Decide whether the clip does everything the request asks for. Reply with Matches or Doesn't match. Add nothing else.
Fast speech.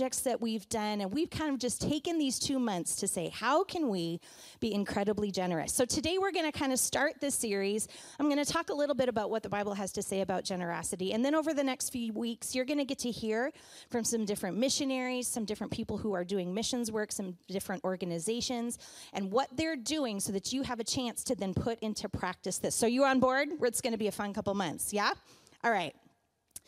Matches